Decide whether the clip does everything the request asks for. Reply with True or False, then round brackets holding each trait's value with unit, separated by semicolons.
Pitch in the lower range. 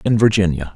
True (95 Hz)